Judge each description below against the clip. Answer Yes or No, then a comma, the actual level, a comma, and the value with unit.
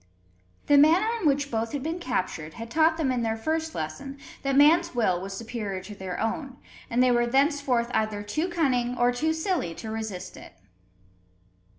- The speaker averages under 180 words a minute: No, average, 185 wpm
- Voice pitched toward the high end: Yes, high, 245 Hz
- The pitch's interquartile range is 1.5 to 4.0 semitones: No, wide, 5.6 semitones